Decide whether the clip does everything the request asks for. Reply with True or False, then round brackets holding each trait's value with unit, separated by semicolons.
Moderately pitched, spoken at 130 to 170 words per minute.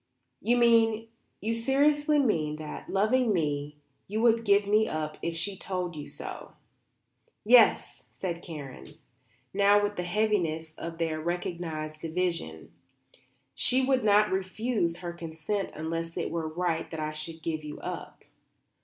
True (175 Hz; 145 wpm)